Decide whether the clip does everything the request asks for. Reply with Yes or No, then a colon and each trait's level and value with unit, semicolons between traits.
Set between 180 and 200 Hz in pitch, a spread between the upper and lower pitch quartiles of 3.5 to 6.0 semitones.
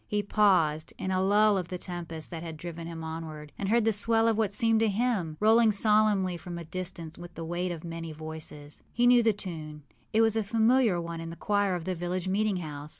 Yes: medium, 185 Hz; average, 4.4 semitones